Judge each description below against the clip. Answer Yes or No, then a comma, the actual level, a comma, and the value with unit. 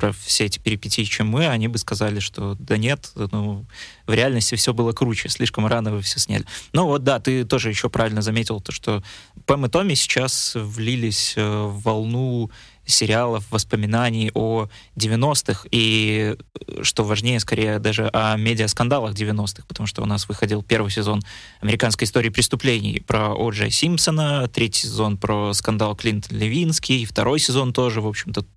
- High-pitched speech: No, low, 110 Hz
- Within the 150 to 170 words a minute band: Yes, fast, 160 wpm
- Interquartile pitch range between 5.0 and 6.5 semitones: No, narrow, 2.5 semitones